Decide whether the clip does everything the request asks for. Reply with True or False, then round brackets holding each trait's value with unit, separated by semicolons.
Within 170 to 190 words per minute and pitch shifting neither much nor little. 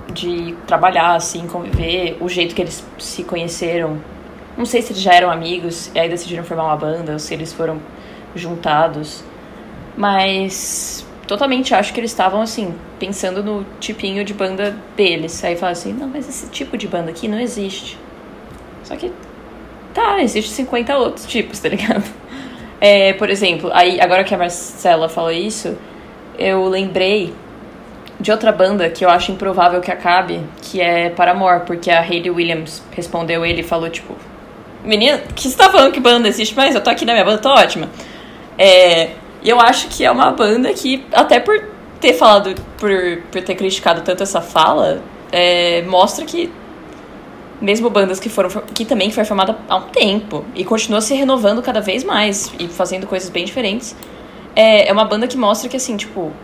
True (180 wpm; 3.9 semitones)